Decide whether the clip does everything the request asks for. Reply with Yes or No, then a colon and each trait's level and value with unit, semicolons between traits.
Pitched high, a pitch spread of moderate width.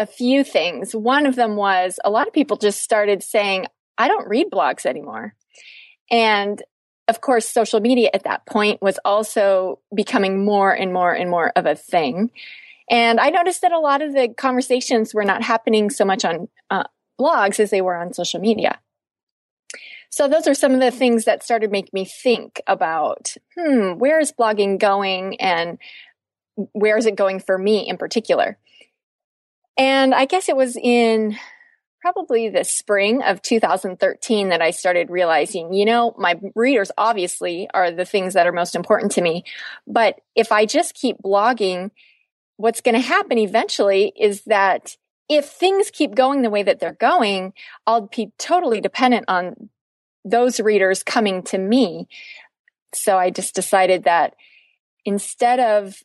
Yes: high, 215 Hz; average, 4.5 semitones